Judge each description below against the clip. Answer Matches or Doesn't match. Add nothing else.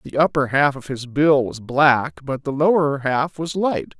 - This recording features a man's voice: Matches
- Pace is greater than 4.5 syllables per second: Doesn't match